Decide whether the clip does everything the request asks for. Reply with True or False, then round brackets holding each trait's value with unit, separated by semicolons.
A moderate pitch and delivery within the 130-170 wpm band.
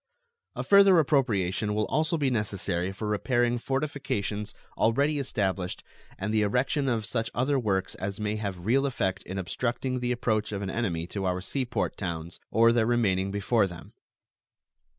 False (110 Hz; 165 wpm)